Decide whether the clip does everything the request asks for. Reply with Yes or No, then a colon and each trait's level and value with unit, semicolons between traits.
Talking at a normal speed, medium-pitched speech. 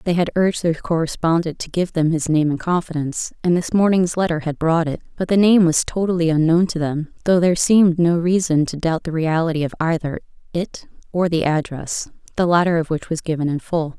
No: fast, 215 wpm; medium, 165 Hz